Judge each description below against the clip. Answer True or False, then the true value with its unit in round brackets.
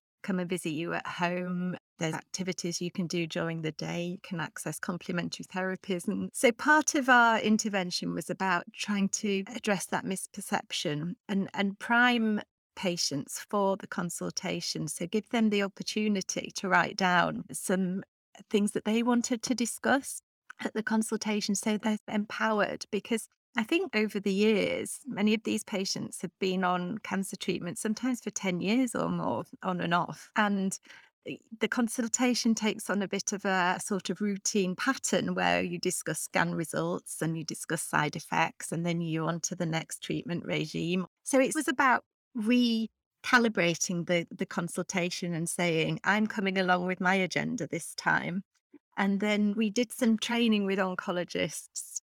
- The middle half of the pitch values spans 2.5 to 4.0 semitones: True (3.7 semitones)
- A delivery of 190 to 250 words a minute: False (165 wpm)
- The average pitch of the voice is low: False (195 Hz)